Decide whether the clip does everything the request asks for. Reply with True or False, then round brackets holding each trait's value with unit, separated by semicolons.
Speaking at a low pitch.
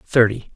True (115 Hz)